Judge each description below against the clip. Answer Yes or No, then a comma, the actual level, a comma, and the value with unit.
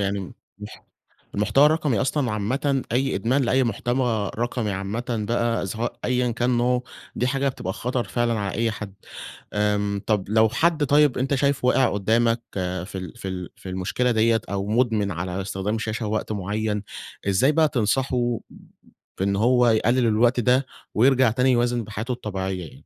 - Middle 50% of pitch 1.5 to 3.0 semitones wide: No, average, 3.6 semitones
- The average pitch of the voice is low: Yes, low, 115 Hz